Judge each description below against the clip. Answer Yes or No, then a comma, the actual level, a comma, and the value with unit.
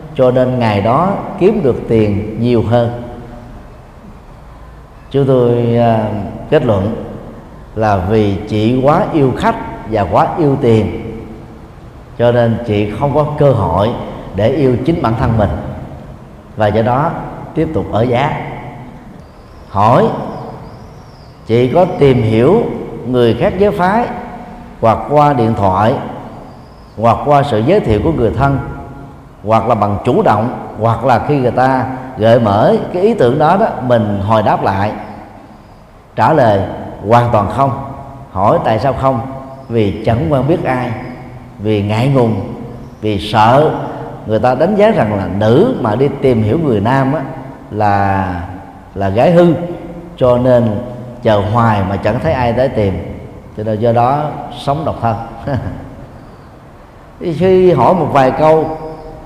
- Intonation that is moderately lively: Yes, average, 4.4 semitones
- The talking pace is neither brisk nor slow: No, slow, 145 wpm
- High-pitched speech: No, low, 120 Hz